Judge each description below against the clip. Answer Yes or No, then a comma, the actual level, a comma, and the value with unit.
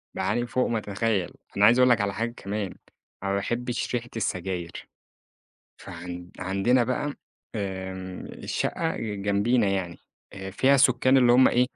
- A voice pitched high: No, low, 105 Hz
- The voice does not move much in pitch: No, average, 4.1 semitones